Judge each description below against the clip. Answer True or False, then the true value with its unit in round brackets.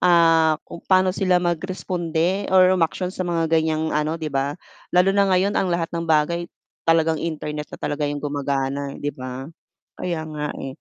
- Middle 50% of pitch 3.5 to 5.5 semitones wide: False (3.1 semitones)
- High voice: False (165 Hz)